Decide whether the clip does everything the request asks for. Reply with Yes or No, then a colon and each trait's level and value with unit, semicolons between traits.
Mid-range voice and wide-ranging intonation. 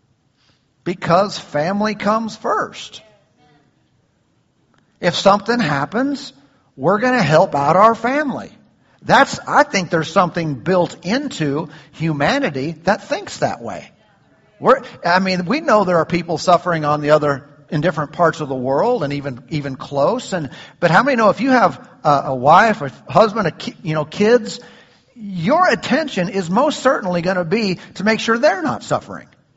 Yes: medium, 180 Hz; wide, 6.6 semitones